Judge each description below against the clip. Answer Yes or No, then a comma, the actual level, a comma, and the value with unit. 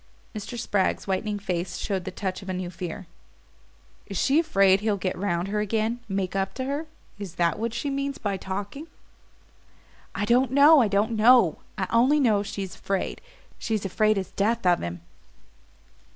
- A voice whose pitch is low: No, high, 205 Hz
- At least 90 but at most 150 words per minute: No, average, 180 wpm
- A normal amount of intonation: Yes, average, 3.7 semitones